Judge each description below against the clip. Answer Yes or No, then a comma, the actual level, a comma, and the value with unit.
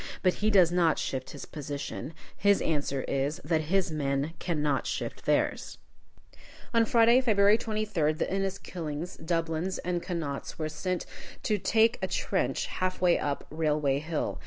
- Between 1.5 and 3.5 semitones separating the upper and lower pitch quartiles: No, average, 4.4 semitones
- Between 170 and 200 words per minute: No, average, 155 wpm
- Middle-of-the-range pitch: Yes, medium, 170 Hz